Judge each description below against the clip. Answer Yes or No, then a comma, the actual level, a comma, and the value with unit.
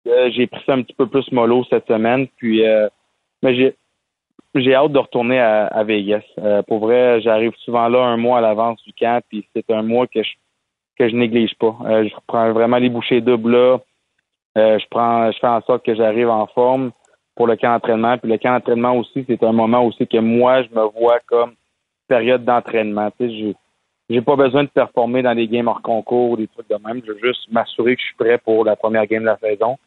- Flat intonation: Yes, narrow, 2.0 semitones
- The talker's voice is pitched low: Yes, low, 115 Hz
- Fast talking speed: Yes, fast, 230 wpm